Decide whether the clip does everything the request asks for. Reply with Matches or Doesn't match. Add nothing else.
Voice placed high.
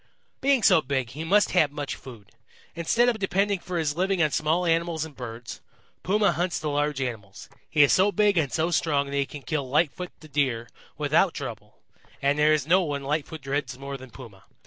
Doesn't match